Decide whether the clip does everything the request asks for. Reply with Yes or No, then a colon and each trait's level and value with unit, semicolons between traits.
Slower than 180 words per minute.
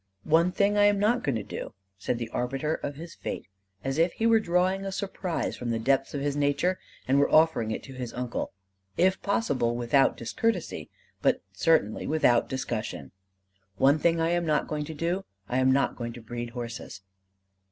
No: average, 195 wpm